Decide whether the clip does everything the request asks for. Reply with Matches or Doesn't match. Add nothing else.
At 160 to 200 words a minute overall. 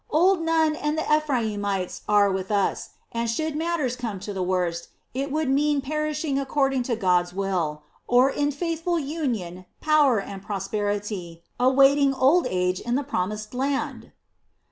Doesn't match